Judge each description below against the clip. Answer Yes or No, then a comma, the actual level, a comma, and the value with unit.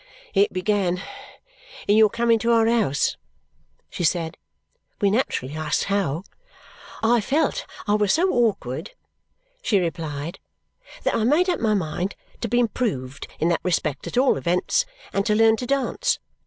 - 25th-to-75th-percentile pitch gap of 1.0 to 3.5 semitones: No, wide, 5.6 semitones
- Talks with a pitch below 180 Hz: No, high, 205 Hz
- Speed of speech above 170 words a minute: No, average, 155 wpm